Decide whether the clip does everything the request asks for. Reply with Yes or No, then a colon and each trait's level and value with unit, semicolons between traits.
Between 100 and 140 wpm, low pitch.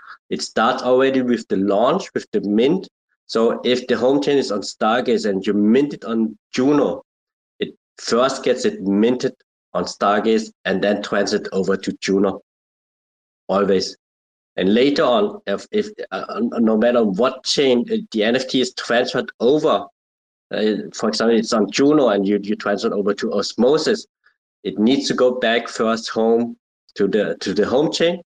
No: average, 170 wpm; low, 115 Hz